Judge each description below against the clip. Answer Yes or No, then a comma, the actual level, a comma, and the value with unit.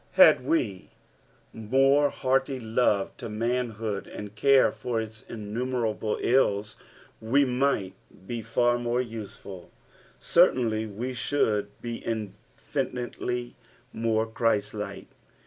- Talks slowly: Yes, slow, 105 wpm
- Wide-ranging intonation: No, average, 2.8 semitones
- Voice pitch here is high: No, low, 115 Hz